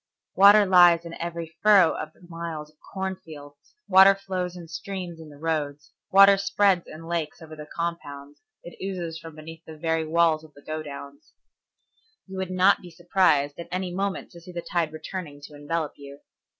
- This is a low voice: No, medium, 170 Hz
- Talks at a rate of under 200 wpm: Yes, average, 185 wpm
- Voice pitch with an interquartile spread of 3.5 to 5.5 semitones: No, average, 3.0 semitones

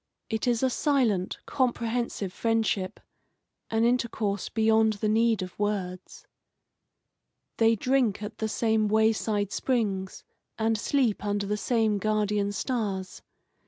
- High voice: Yes, high, 220 Hz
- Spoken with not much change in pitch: Yes, narrow, 2.1 semitones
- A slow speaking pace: Yes, slow, 125 wpm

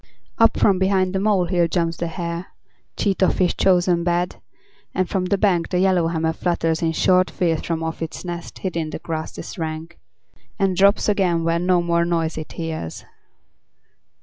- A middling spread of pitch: No, narrow, 2.1 semitones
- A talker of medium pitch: Yes, medium, 175 Hz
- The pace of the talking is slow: No, average, 175 wpm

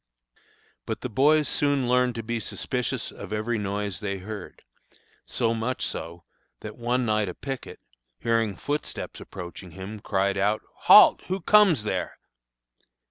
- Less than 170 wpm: Yes, average, 140 wpm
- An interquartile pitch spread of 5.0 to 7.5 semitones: No, average, 3.9 semitones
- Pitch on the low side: Yes, low, 110 Hz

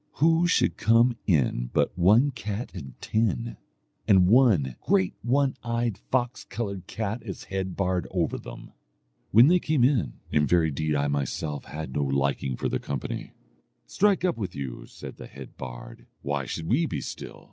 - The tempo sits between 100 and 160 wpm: No, average, 170 wpm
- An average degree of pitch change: No, wide, 9.0 semitones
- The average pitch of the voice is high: No, very low, 95 Hz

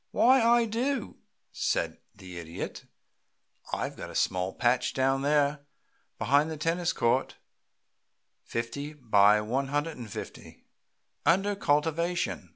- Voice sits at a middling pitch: Yes, medium, 145 Hz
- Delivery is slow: Yes, slow, 115 wpm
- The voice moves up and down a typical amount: No, wide, 5.9 semitones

